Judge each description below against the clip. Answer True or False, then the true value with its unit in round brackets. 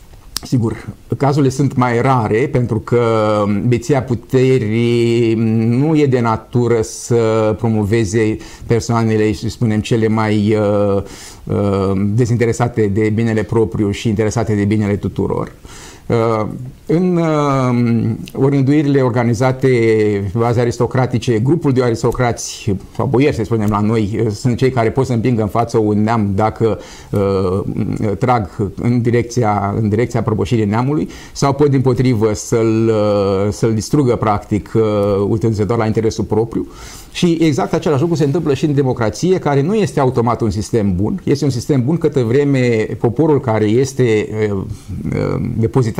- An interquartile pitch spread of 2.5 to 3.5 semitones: True (3.0 semitones)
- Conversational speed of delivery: True (135 wpm)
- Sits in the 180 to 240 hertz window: False (115 Hz)